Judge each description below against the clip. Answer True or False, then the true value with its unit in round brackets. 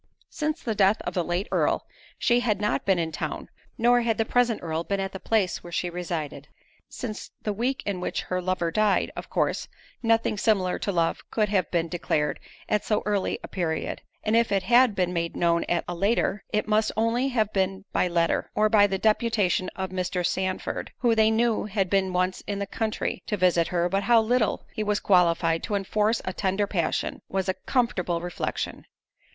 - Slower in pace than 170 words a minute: False (200 wpm)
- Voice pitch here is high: True (195 Hz)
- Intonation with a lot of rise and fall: False (3.4 semitones)